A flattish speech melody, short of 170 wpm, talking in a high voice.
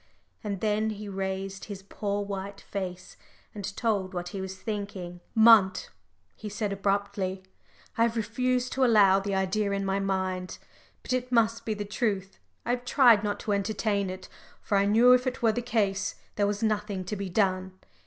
No: narrow, 2.3 semitones; average, 185 wpm; high, 200 Hz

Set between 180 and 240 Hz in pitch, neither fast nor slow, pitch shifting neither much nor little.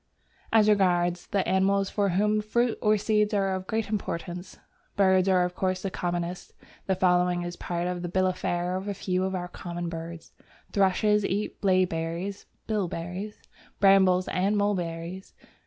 No: medium, 185 Hz; average, 160 wpm; narrow, 2.2 semitones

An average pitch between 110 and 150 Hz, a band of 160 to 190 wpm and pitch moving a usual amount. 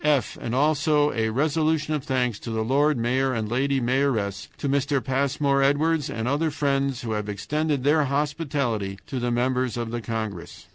Yes: low, 135 Hz; average, 180 wpm; average, 3.7 semitones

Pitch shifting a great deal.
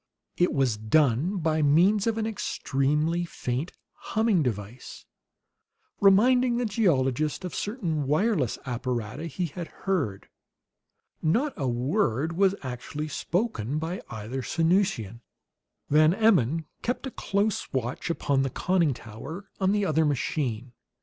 Yes: wide, 6.9 semitones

